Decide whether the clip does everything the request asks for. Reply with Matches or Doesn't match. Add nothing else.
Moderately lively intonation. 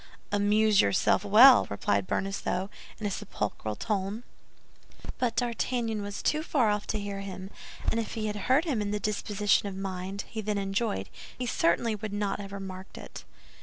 Doesn't match